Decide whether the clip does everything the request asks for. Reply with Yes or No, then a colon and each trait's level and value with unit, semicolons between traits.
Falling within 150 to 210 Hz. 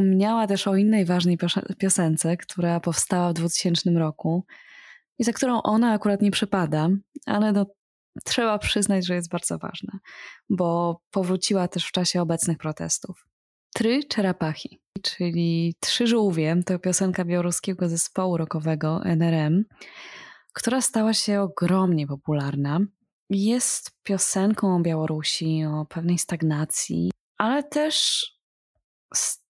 Yes: medium, 185 Hz